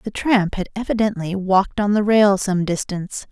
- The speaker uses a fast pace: No, average, 180 wpm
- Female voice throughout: Yes, female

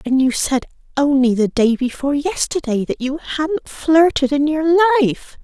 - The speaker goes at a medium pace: Yes, average, 165 wpm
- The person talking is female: Yes, female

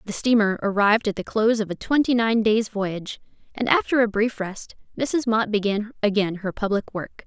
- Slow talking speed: No, average, 200 wpm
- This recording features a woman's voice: Yes, female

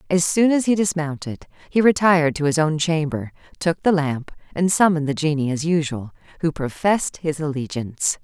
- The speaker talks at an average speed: Yes, average, 175 wpm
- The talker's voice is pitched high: No, medium, 160 Hz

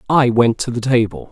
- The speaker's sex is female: No, male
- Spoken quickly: Yes, fast, 230 wpm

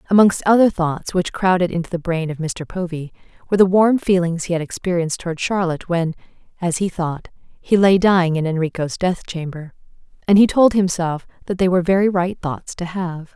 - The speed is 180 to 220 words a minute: Yes, average, 195 wpm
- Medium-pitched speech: Yes, medium, 180 Hz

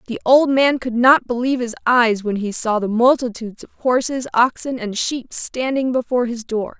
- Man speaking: No, female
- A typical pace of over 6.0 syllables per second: No, 5.0 syllables/s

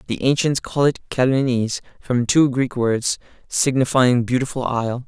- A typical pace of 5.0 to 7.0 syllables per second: Yes, 5.1 syllables/s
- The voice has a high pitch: No, low, 125 Hz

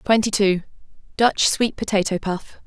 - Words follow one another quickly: No, slow, 115 wpm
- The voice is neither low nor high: No, high, 205 Hz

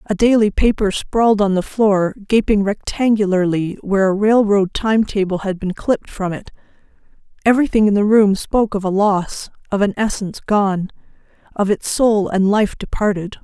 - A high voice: Yes, high, 205 Hz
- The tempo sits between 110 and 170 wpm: Yes, average, 165 wpm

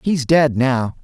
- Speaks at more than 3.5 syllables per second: No, 3.3 syllables/s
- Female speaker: No, male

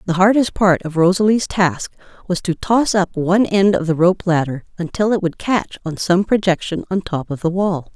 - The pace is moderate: No, fast, 210 wpm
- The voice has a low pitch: No, medium, 185 Hz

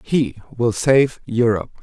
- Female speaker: No, male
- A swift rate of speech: No, slow, 130 wpm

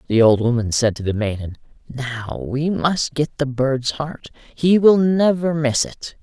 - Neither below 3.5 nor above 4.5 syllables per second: Yes, 4.0 syllables/s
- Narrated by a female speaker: No, male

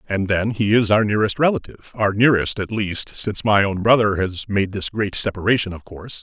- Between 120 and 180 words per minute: No, average, 200 wpm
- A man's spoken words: Yes, male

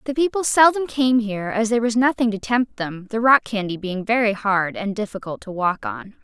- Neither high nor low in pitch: No, high, 220 Hz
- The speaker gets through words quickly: Yes, fast, 220 wpm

